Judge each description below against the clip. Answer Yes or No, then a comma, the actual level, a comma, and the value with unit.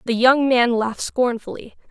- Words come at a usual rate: Yes, average, 155 wpm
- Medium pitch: No, high, 240 Hz